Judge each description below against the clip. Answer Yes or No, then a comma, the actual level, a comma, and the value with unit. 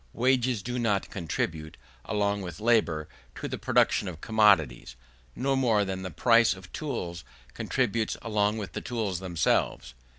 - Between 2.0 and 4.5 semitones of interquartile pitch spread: No, average, 5.0 semitones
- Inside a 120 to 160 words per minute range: Yes, average, 145 wpm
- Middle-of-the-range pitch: No, low, 105 Hz